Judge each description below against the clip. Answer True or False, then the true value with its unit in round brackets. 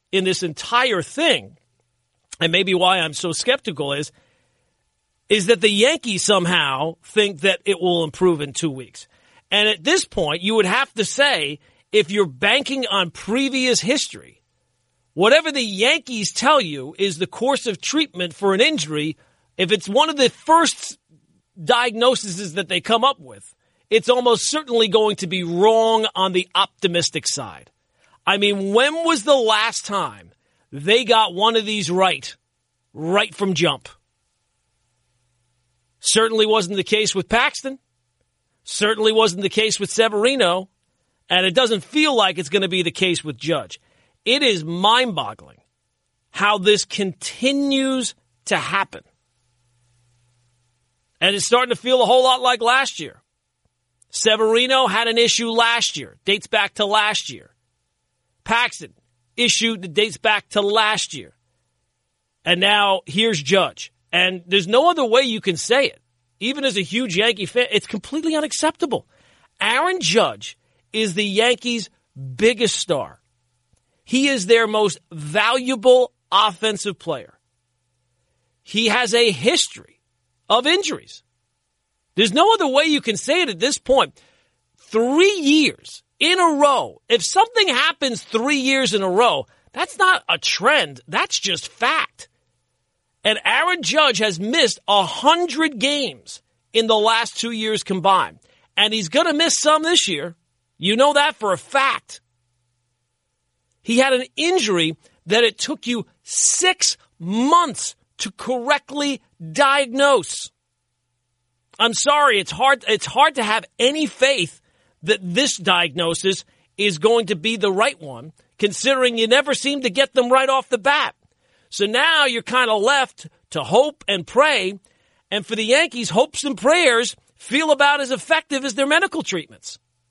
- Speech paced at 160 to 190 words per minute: False (150 wpm)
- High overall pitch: True (210 Hz)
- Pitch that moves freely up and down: True (7.7 semitones)